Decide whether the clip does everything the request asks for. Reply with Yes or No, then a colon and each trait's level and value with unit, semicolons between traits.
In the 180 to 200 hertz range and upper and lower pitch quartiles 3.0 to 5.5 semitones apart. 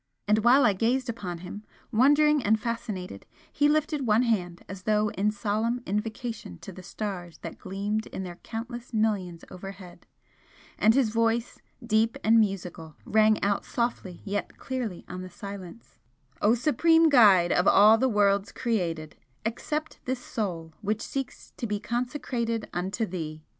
No: high, 215 Hz; average, 3.9 semitones